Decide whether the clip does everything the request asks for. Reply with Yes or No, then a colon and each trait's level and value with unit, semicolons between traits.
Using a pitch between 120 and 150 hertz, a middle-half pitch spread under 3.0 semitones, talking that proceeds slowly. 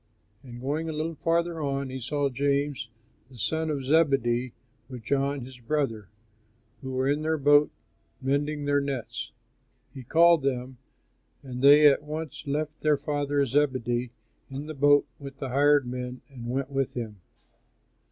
No: medium, 140 Hz; narrow, 2.4 semitones; average, 155 wpm